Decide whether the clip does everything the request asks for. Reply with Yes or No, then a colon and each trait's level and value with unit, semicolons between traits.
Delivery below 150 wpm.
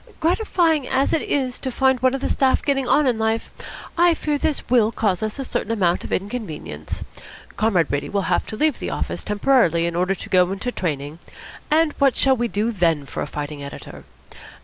No: fast, 205 wpm